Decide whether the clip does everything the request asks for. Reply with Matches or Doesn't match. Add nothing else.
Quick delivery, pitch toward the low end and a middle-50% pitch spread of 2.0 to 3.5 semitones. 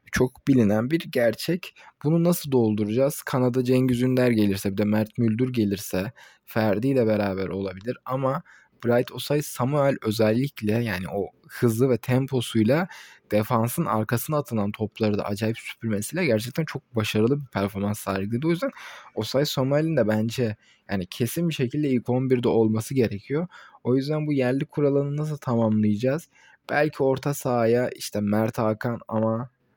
Doesn't match